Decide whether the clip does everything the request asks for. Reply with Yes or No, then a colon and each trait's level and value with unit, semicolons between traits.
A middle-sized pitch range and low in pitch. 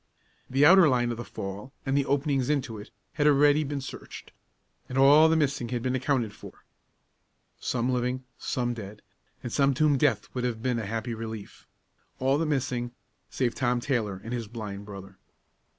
Yes: average, 3.5 semitones; low, 125 Hz